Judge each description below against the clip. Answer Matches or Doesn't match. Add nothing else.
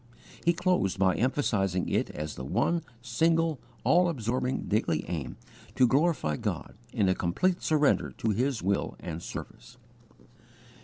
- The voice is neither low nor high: Doesn't match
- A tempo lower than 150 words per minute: Matches